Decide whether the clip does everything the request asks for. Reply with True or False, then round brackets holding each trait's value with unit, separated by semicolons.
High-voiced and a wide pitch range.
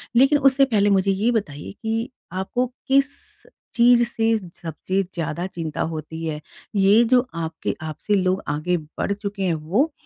True (195 Hz; 6.2 semitones)